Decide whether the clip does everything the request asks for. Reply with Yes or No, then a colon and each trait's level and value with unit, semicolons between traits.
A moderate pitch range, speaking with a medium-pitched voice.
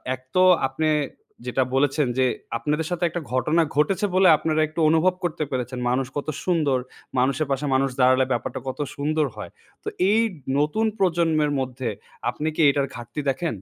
Yes: average, 3.6 semitones; medium, 150 Hz